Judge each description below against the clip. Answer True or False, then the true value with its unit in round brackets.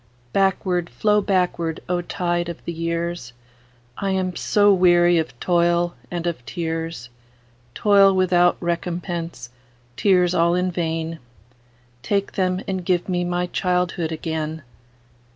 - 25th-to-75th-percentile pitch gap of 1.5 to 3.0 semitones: True (2.5 semitones)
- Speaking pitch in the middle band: True (170 Hz)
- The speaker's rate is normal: False (115 wpm)